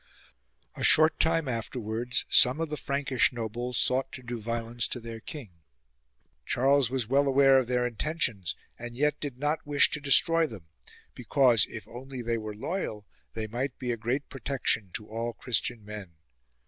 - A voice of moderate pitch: No, low, 125 Hz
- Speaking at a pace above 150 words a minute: Yes, average, 170 wpm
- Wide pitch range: No, average, 3.5 semitones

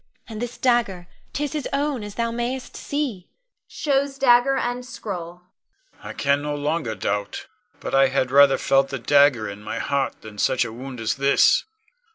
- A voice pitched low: No, medium, 170 Hz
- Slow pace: No, average, 185 wpm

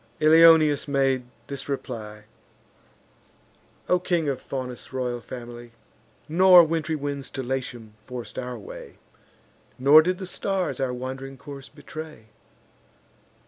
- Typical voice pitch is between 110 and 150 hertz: Yes, low, 135 Hz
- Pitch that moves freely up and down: No, average, 4.0 semitones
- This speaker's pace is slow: Yes, slow, 115 wpm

